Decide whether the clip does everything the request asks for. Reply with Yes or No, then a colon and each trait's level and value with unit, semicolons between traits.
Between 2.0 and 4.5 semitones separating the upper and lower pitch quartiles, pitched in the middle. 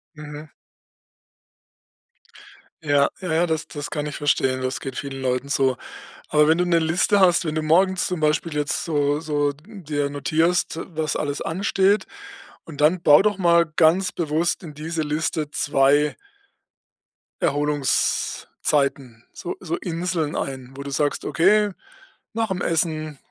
Yes: average, 2.8 semitones; medium, 155 Hz